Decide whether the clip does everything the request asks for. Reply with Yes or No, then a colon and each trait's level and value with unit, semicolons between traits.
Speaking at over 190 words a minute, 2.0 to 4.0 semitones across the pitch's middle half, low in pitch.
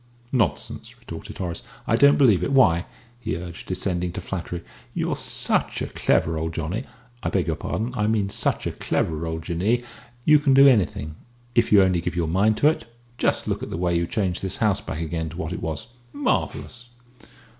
No: average, 200 wpm; average, 5.1 semitones; very low, 90 Hz